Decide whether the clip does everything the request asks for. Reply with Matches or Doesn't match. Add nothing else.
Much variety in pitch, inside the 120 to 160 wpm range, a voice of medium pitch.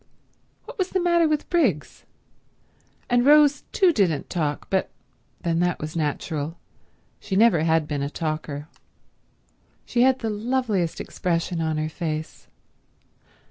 Matches